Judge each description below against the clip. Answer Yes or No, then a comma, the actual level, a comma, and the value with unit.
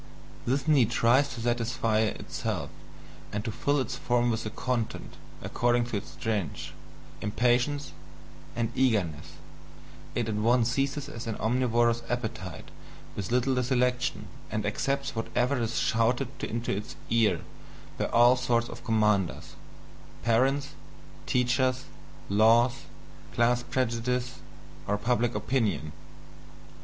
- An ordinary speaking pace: No, slow, 120 wpm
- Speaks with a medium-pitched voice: No, low, 120 Hz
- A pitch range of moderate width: No, narrow, 2.2 semitones